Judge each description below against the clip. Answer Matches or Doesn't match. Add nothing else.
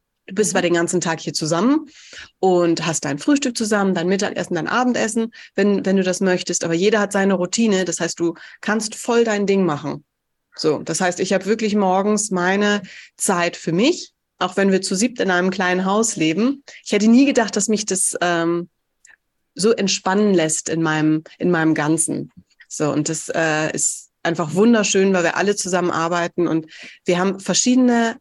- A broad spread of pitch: Doesn't match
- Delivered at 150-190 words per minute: Matches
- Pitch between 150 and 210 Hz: Matches